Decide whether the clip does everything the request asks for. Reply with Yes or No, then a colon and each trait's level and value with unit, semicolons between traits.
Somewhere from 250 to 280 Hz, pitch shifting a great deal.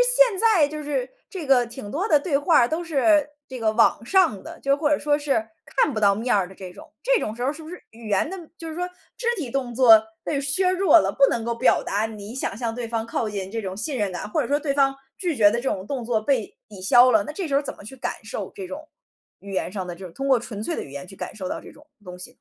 Yes: very high, 255 Hz; wide, 6.0 semitones